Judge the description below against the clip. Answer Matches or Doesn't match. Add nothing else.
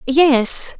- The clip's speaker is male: Doesn't match